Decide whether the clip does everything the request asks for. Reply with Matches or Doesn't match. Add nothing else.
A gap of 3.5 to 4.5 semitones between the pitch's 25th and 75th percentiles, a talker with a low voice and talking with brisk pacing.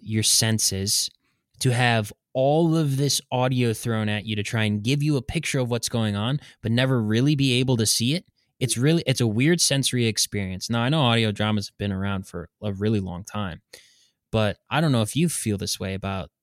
Matches